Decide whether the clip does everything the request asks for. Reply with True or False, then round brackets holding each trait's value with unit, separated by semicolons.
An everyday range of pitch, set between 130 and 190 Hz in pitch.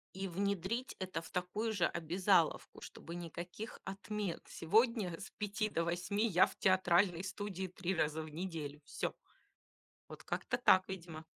True (3.0 semitones; 185 Hz)